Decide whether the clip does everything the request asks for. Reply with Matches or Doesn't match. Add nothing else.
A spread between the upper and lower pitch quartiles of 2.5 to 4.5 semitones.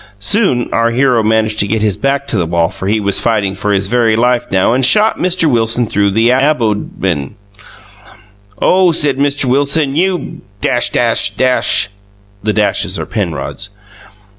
Doesn't match